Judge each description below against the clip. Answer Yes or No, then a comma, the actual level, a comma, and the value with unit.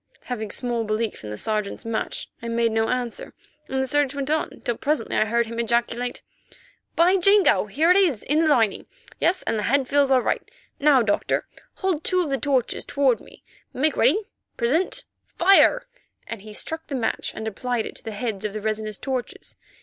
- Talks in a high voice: Yes, very high, 250 Hz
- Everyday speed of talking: Yes, average, 195 wpm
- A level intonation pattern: No, average, 4.9 semitones